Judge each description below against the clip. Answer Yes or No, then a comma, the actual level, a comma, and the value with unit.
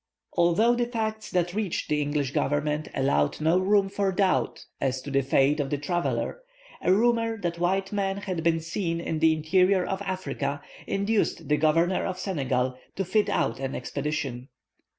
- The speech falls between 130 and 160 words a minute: No, average, 170 wpm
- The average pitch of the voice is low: No, medium, 170 Hz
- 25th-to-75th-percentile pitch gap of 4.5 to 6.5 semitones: Yes, average, 4.9 semitones